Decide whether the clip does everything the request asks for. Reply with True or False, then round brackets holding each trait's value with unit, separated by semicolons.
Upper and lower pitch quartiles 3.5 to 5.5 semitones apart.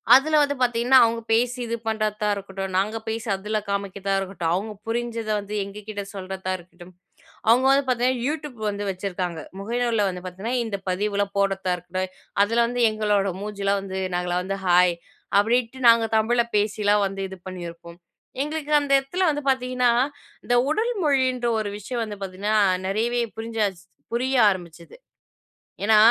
True (3.8 semitones)